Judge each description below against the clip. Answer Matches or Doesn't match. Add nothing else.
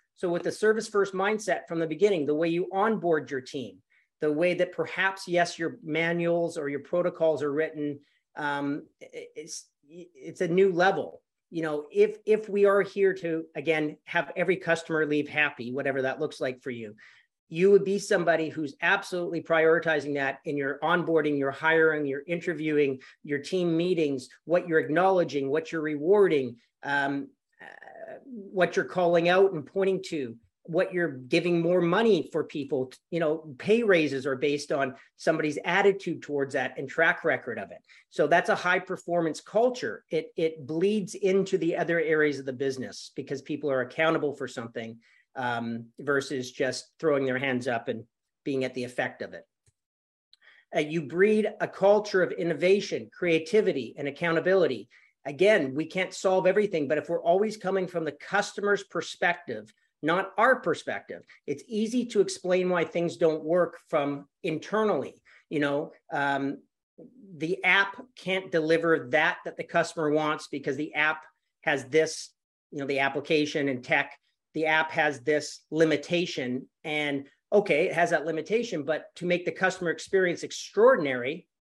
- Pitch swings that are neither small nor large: Matches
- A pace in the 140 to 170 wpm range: Matches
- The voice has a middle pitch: Matches